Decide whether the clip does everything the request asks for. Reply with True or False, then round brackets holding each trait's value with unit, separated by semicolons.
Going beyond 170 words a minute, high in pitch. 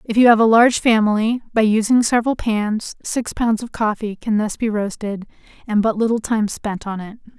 True (205 wpm; 220 Hz)